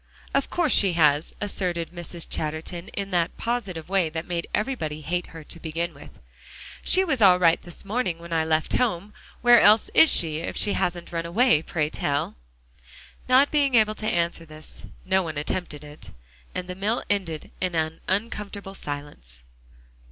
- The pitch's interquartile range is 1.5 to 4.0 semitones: No, average, 4.4 semitones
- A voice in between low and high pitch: Yes, medium, 175 Hz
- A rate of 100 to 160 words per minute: No, average, 175 wpm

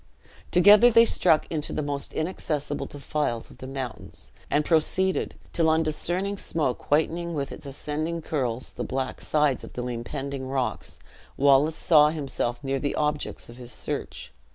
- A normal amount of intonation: Yes, average, 3.1 semitones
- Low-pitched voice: No, medium, 150 Hz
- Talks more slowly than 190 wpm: Yes, average, 155 wpm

